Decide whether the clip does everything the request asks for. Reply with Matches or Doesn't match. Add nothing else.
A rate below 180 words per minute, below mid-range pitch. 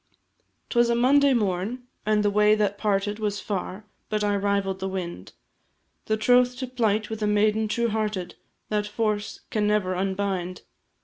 Doesn't match